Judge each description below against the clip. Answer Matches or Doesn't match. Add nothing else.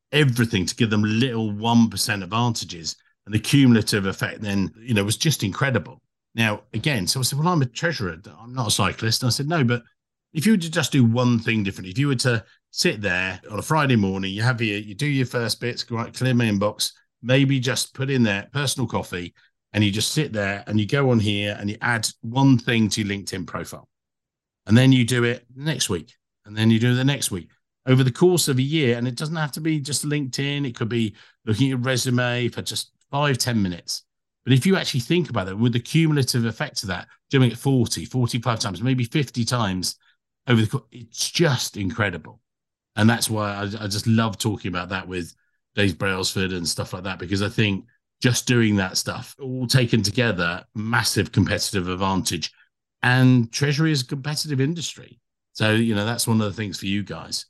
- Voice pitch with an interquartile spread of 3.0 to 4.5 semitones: Matches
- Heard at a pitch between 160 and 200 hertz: Doesn't match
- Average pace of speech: Doesn't match